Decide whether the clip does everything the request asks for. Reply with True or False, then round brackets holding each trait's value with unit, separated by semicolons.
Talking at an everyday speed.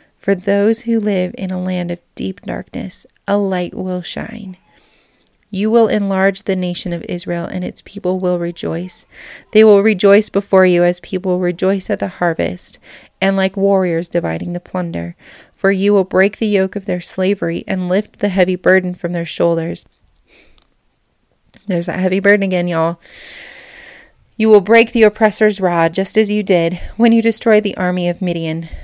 True (175 wpm)